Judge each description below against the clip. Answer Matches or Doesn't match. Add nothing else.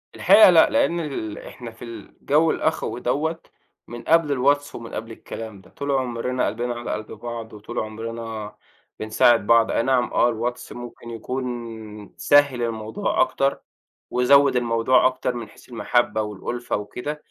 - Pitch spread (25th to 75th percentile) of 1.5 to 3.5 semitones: Matches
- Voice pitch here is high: Doesn't match